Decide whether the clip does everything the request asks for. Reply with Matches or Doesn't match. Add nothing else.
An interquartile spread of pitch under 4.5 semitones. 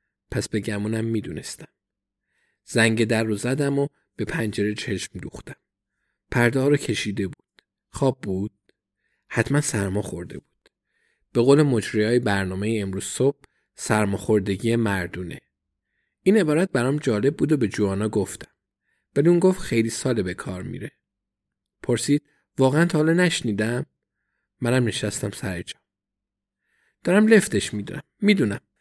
Doesn't match